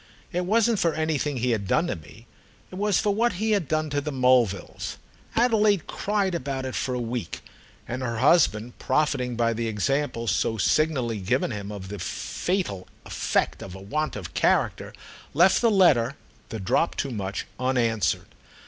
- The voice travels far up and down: Yes, wide, 7.2 semitones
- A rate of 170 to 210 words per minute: Yes, average, 175 wpm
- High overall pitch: No, low, 130 Hz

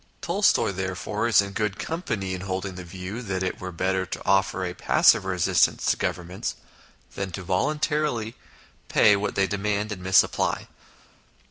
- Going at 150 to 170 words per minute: Yes, average, 160 wpm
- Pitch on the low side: Yes, very low, 95 Hz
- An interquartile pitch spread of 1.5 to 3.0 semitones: Yes, narrow, 2.5 semitones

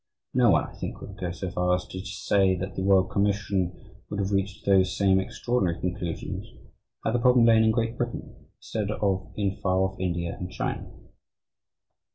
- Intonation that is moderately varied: No, narrow, 1.8 semitones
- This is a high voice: No, very low, 95 Hz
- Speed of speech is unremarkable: Yes, average, 185 wpm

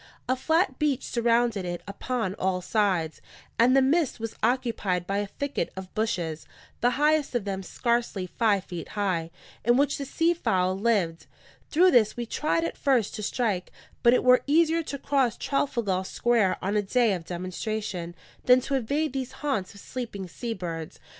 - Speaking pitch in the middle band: No, high, 230 Hz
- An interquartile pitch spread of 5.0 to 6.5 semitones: Yes, wide, 5.6 semitones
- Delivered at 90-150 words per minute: No, average, 175 wpm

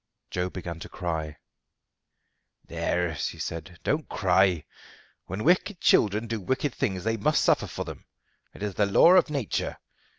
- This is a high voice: No, low, 100 Hz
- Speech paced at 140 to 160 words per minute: Yes, average, 155 wpm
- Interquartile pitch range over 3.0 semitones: Yes, wide, 5.6 semitones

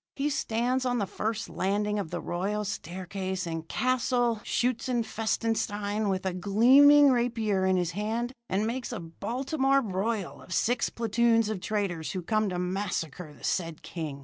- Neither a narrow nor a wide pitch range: Yes, average, 4.1 semitones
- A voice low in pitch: No, high, 210 Hz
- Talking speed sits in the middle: Yes, average, 155 wpm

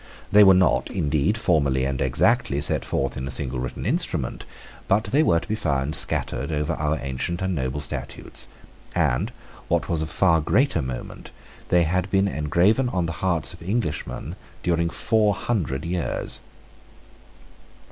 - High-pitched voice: No, very low, 85 Hz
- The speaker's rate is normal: Yes, average, 155 wpm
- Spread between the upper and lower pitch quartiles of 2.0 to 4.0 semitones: No, wide, 5.5 semitones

